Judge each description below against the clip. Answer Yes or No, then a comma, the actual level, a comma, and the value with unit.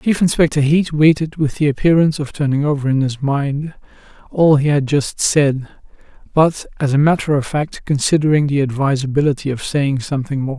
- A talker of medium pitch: Yes, medium, 145 Hz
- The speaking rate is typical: Yes, average, 175 wpm